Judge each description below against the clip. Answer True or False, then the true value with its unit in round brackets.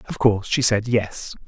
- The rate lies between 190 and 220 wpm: True (205 wpm)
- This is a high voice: False (110 Hz)